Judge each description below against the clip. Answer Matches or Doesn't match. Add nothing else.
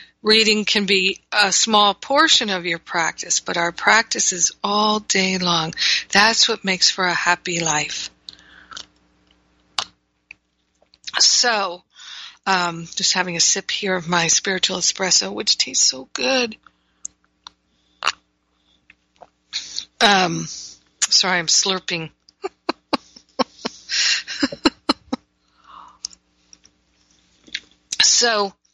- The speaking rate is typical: Doesn't match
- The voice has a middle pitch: Matches